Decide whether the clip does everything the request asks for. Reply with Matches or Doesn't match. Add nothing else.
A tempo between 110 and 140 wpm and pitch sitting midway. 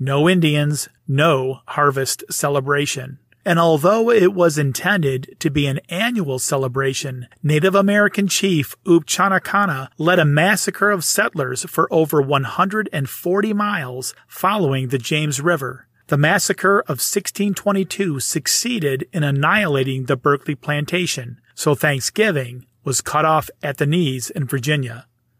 Matches